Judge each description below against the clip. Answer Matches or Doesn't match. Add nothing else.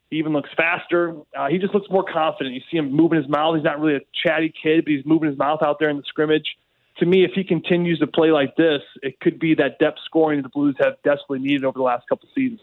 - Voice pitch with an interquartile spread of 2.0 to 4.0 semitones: Matches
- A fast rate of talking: Matches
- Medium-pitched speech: Matches